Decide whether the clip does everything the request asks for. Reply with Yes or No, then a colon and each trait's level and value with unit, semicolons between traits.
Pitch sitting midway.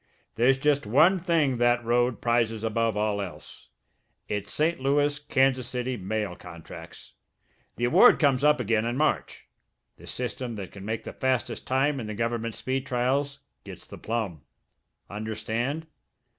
No: low, 120 Hz